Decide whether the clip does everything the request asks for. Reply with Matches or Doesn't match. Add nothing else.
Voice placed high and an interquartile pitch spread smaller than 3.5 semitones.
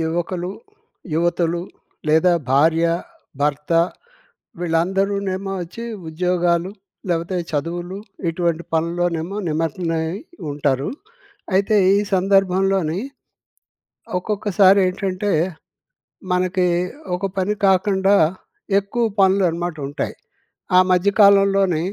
Doesn't match